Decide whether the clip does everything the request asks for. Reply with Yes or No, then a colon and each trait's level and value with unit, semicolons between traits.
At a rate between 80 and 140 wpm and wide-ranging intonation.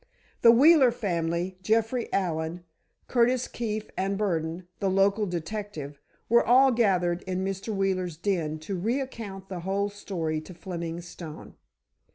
No: slow, 135 wpm; average, 4.1 semitones